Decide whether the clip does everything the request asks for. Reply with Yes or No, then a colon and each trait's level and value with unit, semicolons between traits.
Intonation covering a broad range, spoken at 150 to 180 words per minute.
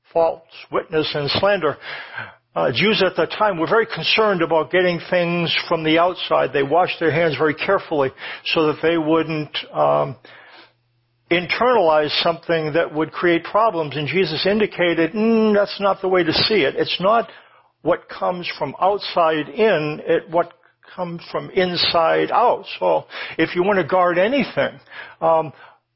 No: average, 3.0 semitones; average, 155 wpm